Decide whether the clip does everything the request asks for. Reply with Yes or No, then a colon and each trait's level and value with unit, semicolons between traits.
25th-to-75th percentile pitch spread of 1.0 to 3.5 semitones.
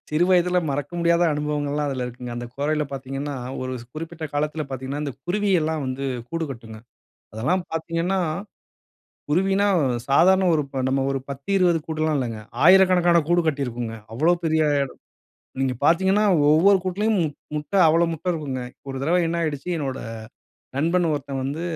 No: average, 4.1 semitones